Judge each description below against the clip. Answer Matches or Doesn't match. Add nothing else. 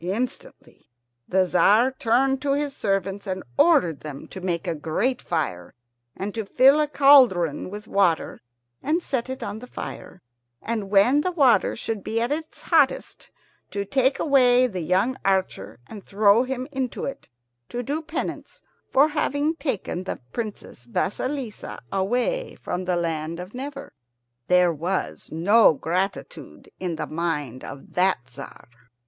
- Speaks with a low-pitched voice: Doesn't match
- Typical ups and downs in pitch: Doesn't match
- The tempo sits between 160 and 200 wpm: Doesn't match